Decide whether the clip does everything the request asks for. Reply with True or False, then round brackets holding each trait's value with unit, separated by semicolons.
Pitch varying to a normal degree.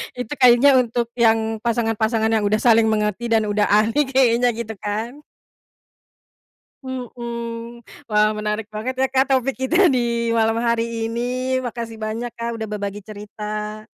False (2.1 semitones)